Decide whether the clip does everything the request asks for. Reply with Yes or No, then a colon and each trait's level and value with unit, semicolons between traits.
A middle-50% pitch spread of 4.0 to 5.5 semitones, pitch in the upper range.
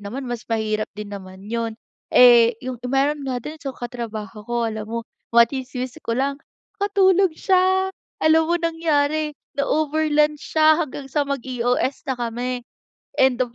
Yes: average, 4.8 semitones; very high, 265 Hz